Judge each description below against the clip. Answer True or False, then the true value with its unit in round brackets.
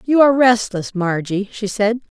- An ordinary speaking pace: True (165 wpm)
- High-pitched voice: True (215 Hz)